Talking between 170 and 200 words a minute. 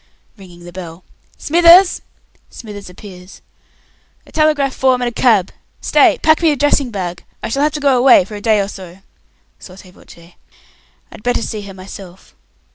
No: average, 160 wpm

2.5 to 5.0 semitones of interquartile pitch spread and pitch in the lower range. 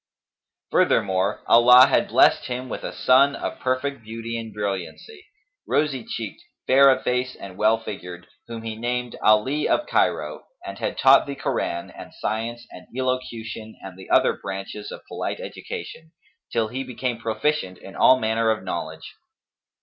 Yes: average, 3.4 semitones; low, 115 Hz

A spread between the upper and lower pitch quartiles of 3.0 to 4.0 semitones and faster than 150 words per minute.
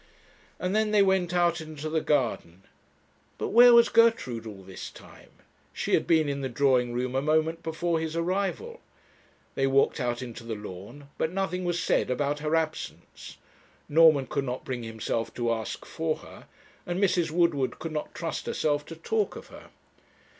No: wide, 5.5 semitones; average, 175 wpm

